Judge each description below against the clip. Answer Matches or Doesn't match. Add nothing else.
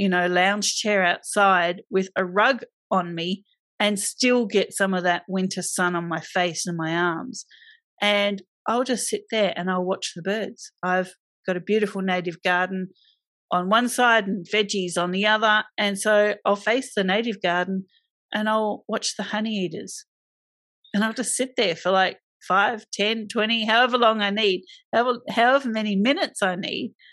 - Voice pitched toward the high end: Matches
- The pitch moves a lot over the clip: Doesn't match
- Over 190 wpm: Doesn't match